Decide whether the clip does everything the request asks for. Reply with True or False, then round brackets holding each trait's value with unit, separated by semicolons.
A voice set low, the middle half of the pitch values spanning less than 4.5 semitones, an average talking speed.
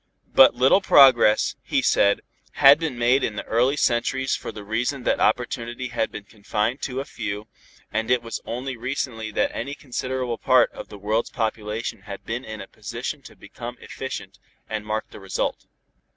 True (120 Hz; 3.1 semitones; 180 wpm)